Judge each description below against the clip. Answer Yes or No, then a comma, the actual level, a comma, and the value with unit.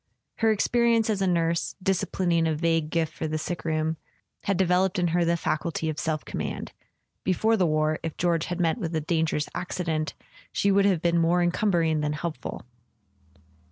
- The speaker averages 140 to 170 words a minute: No, average, 180 wpm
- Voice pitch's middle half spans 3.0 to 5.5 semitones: No, narrow, 2.6 semitones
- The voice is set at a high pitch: No, medium, 170 Hz